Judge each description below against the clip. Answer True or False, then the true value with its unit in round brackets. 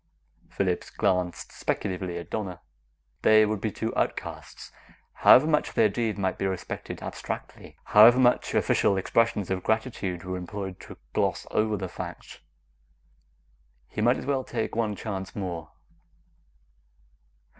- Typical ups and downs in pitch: True (3.2 semitones)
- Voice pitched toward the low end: True (105 Hz)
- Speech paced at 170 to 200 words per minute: False (135 wpm)